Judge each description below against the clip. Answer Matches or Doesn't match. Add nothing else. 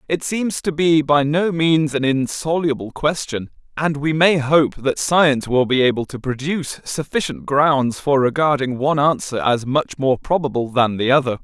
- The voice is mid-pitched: Matches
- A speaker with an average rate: Matches